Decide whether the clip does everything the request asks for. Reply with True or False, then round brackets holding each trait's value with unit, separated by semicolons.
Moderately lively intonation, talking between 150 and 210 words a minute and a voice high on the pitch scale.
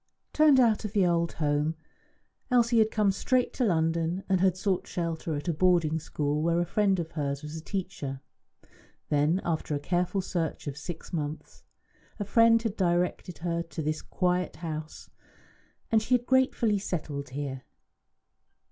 False (4.4 semitones; 165 wpm; 175 Hz)